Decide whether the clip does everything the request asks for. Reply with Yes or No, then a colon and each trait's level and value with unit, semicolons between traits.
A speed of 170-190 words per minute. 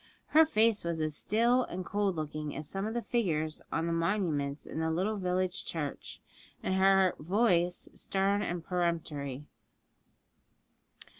No: average, 145 wpm